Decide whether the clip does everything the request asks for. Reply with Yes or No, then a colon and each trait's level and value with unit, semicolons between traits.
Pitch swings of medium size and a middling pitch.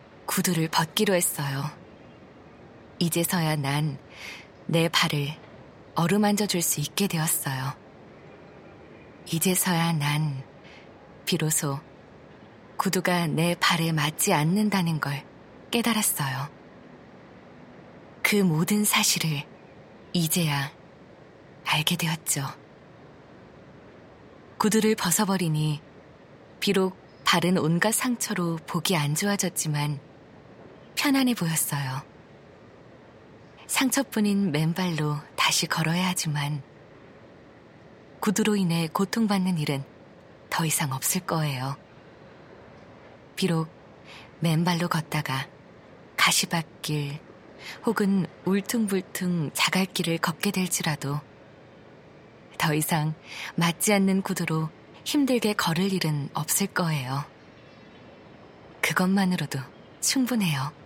Yes: average, 4.1 semitones; medium, 170 Hz